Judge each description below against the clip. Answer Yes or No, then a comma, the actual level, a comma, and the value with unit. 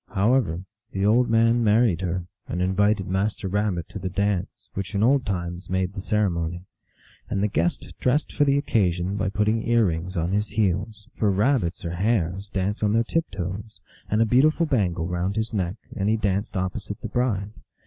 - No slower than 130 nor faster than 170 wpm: No, average, 190 wpm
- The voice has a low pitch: Yes, low, 100 Hz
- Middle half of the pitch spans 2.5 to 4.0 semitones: Yes, average, 3.3 semitones